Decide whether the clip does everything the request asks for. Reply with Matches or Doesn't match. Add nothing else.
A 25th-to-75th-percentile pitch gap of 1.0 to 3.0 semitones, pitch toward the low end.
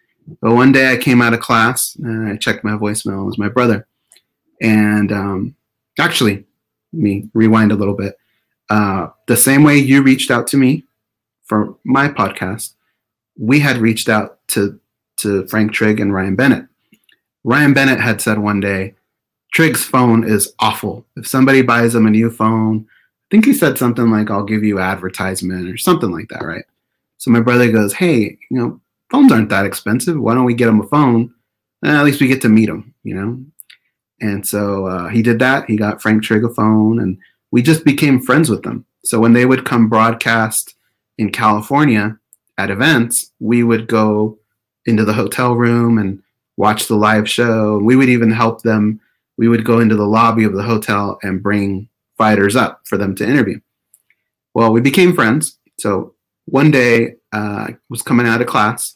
Matches